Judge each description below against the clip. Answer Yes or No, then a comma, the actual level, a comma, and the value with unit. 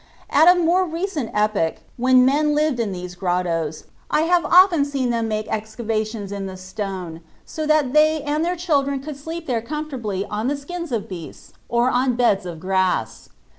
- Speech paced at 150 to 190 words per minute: Yes, average, 180 wpm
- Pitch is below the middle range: No, high, 245 Hz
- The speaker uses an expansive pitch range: Yes, wide, 7.3 semitones